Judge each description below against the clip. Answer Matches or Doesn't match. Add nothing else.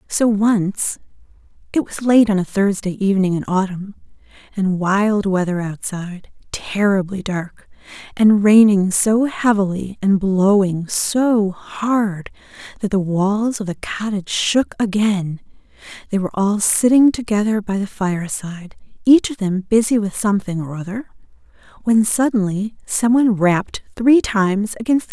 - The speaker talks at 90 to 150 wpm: Matches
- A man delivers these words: Doesn't match